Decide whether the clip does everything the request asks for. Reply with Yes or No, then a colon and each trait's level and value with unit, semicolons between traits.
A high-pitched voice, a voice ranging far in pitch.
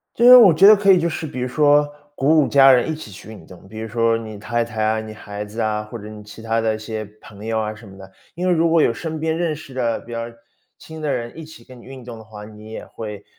No: low, 115 Hz; wide, 6.0 semitones